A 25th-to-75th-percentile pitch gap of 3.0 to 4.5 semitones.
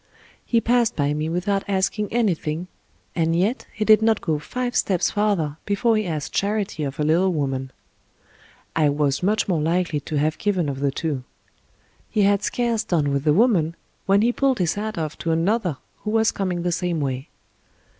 No: wide, 5.6 semitones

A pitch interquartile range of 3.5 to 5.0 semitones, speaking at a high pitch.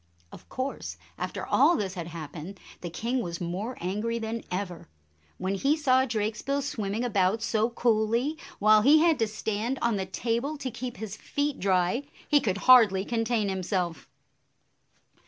Yes: average, 4.6 semitones; high, 220 Hz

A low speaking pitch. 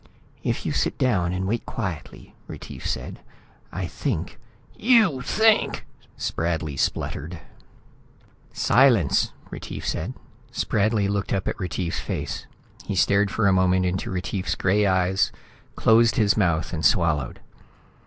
Yes: very low, 95 Hz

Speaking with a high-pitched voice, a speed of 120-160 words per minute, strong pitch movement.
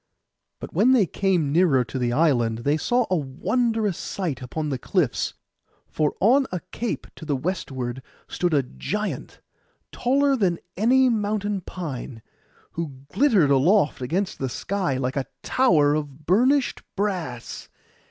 No: medium, 170 Hz; average, 140 wpm; wide, 7.3 semitones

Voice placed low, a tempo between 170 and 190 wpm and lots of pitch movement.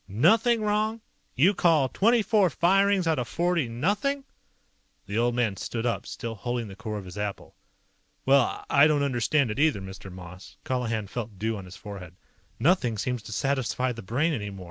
Yes: low, 125 Hz; average, 180 wpm; wide, 7.9 semitones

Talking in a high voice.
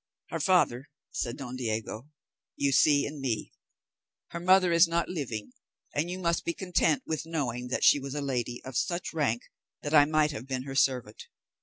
No: medium, 140 Hz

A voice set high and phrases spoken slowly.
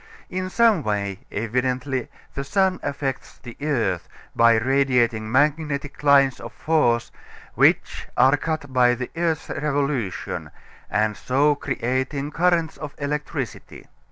No: low, 135 Hz; slow, 120 wpm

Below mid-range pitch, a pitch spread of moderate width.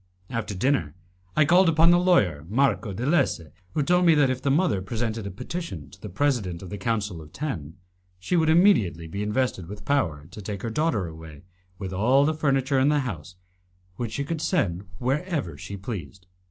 No: low, 115 Hz; wide, 7.8 semitones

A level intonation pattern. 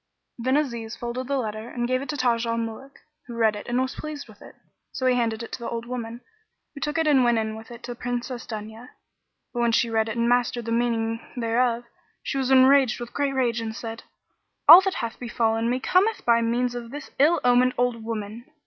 Yes: narrow, 1.9 semitones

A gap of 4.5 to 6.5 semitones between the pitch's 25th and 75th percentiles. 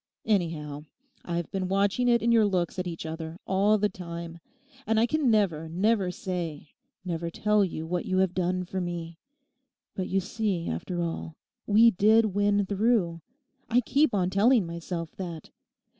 No: average, 3.7 semitones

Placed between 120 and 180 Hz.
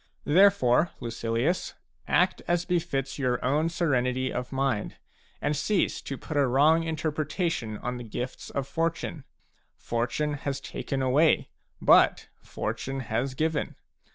Yes: medium, 140 Hz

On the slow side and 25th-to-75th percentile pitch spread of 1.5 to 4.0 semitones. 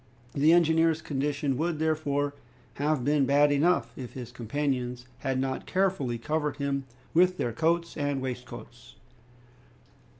Yes: slow, 130 wpm; average, 3.2 semitones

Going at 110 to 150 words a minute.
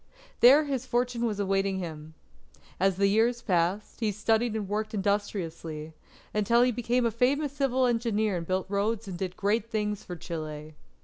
No: average, 170 wpm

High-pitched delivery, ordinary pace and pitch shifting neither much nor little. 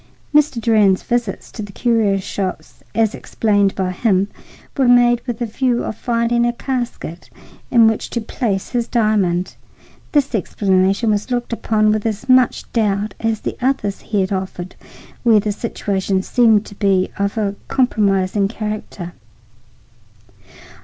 Yes: high, 215 Hz; average, 145 wpm; average, 3.2 semitones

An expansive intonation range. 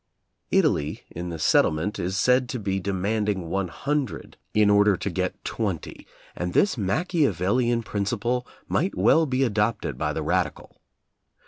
No: average, 4.8 semitones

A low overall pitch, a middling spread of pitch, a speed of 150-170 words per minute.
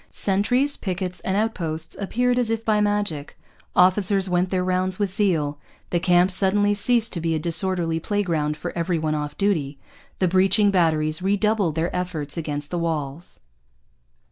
No: medium, 180 Hz; average, 4.0 semitones; average, 160 wpm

